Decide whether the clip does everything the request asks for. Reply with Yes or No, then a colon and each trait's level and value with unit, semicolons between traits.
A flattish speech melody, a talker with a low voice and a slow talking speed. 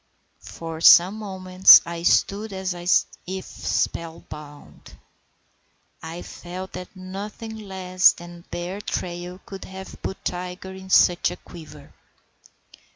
No: narrow, 1.7 semitones; medium, 185 Hz; slow, 120 wpm